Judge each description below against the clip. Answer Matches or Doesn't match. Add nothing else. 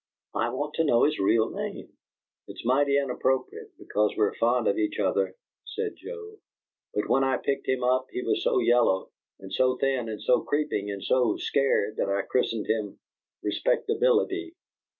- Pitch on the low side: Matches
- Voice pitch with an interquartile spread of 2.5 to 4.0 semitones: Doesn't match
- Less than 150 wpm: Doesn't match